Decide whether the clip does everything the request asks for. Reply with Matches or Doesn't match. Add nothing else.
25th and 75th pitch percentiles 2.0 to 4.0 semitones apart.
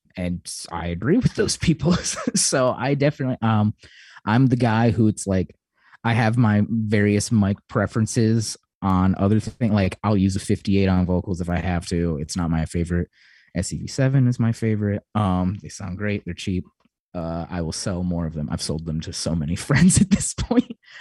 Doesn't match